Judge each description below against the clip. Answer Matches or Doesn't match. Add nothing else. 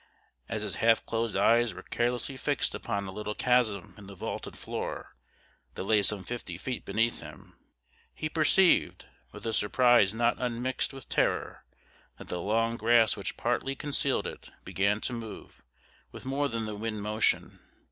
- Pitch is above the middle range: Doesn't match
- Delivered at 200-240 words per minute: Doesn't match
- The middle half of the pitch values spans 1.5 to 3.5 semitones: Matches